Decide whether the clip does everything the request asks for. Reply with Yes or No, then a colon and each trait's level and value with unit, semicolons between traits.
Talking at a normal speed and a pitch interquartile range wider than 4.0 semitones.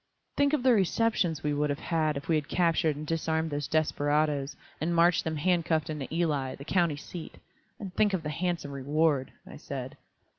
No: average, 190 wpm; average, 2.8 semitones